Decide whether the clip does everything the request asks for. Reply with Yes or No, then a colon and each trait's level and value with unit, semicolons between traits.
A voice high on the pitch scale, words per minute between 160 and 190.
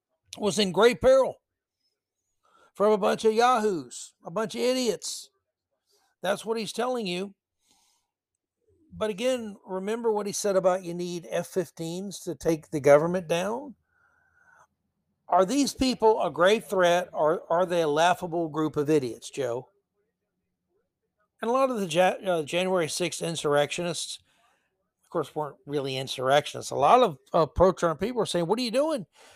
No: high, 195 Hz; average, 145 wpm